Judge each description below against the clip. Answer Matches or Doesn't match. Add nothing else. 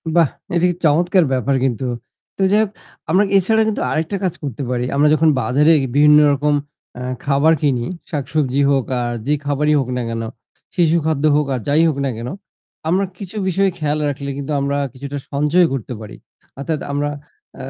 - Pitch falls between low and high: Matches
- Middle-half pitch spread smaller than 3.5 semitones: Matches